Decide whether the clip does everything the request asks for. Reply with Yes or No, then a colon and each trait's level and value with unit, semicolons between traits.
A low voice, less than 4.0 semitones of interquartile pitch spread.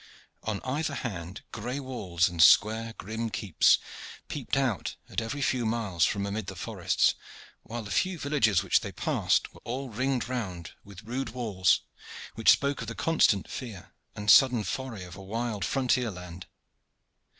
No: low, 115 Hz; average, 4.6 semitones